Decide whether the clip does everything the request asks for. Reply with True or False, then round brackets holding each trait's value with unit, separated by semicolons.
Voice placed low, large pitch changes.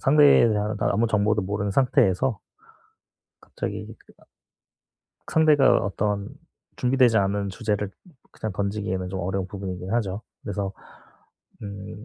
False (105 Hz; 2.3 semitones)